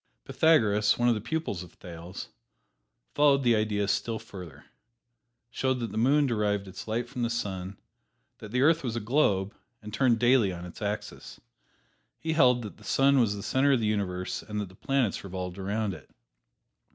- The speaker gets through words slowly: No, average, 185 wpm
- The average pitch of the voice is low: Yes, low, 110 Hz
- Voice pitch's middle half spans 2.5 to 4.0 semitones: No, average, 4.4 semitones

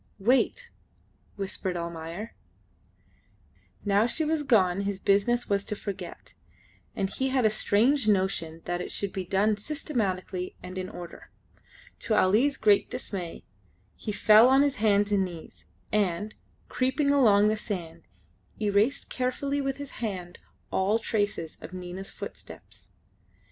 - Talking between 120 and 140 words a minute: Yes, slow, 135 wpm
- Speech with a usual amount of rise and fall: Yes, average, 4.5 semitones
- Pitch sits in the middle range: No, high, 205 Hz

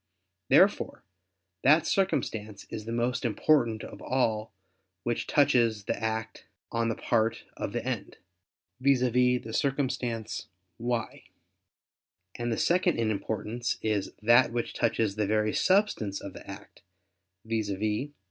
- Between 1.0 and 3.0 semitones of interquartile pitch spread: Yes, narrow, 2.4 semitones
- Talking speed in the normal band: No, slow, 130 wpm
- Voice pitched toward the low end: Yes, low, 115 Hz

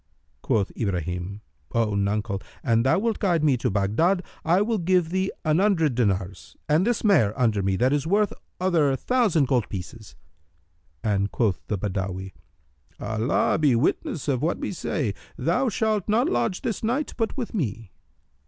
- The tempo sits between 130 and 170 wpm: Yes, average, 160 wpm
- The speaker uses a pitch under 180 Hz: Yes, low, 135 Hz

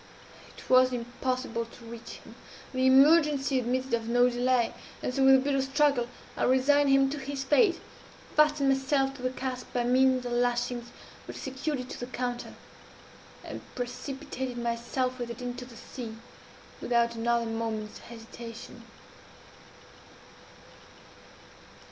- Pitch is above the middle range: Yes, very high, 255 Hz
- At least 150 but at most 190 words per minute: No, average, 140 wpm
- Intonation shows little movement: Yes, narrow, 2.0 semitones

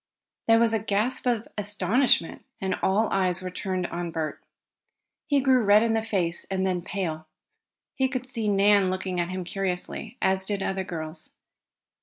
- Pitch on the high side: Yes, high, 195 Hz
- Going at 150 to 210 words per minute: Yes, average, 170 wpm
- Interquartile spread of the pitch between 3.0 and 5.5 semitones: Yes, average, 3.5 semitones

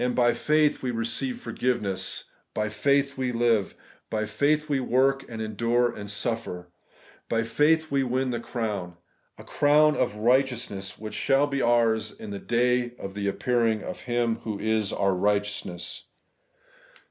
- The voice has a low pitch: Yes, low, 120 Hz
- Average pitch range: Yes, average, 3.8 semitones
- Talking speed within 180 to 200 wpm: No, average, 155 wpm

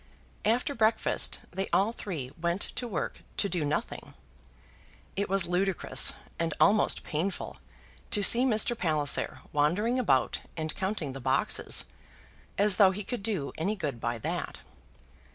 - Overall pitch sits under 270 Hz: Yes, high, 190 Hz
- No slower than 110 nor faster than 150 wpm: Yes, average, 140 wpm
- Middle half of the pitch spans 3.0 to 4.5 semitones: No, wide, 5.4 semitones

